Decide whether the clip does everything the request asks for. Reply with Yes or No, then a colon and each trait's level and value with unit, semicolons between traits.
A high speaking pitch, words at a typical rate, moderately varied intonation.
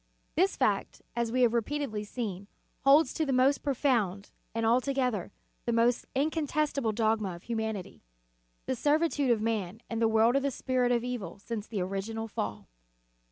Yes: high, 235 Hz; average, 160 wpm; average, 3.9 semitones